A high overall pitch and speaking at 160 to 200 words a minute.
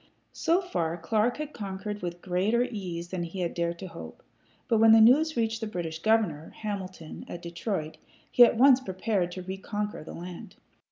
Yes: high, 195 Hz; average, 180 wpm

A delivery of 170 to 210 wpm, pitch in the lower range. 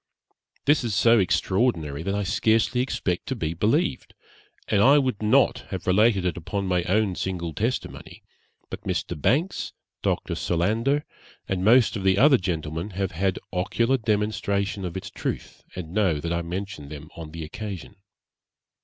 No: average, 160 wpm; low, 100 Hz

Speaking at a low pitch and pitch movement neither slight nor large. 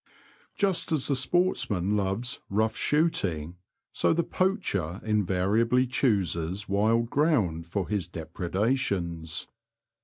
No: low, 105 Hz; wide, 6.2 semitones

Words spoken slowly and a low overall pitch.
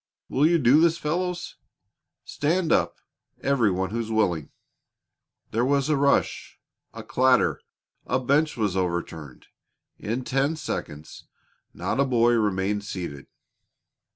Yes: slow, 125 wpm; low, 120 Hz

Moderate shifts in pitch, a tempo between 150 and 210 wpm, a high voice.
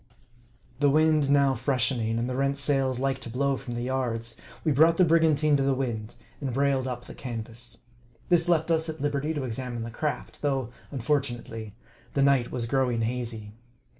No: average, 3.2 semitones; average, 185 wpm; low, 135 Hz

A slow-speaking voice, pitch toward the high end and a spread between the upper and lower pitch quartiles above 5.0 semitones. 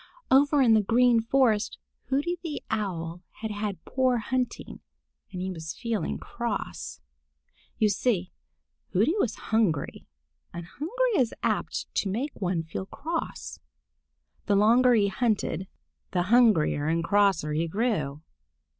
Yes: slow, 130 wpm; high, 210 Hz; wide, 5.6 semitones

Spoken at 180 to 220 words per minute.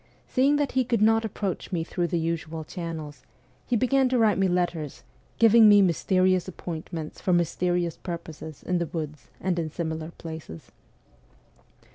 No: average, 155 wpm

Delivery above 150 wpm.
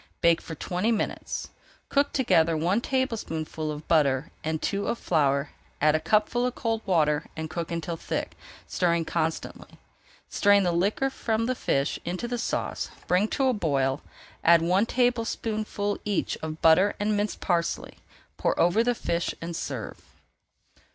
Yes: average, 160 wpm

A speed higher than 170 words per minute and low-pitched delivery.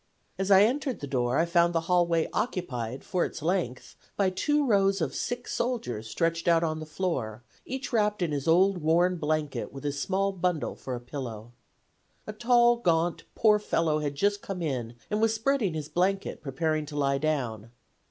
No: average, 180 wpm; medium, 170 Hz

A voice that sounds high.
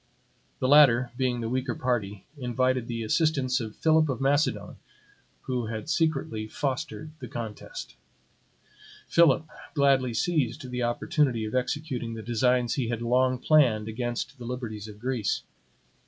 No: low, 125 Hz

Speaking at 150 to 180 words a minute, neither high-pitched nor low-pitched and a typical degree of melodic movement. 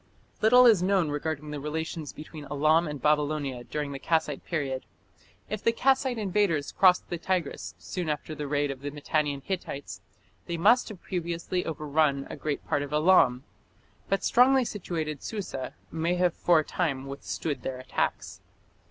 Yes: average, 160 wpm; medium, 155 Hz; average, 4.0 semitones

